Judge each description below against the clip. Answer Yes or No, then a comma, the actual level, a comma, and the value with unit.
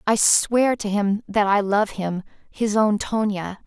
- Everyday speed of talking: Yes, average, 180 wpm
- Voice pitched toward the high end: Yes, high, 210 Hz